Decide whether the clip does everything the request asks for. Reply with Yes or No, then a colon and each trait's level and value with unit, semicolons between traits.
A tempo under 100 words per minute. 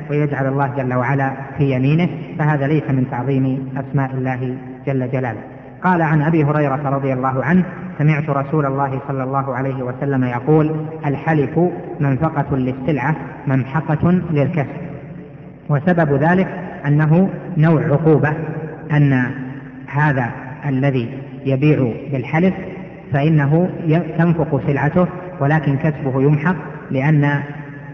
No: average, 110 wpm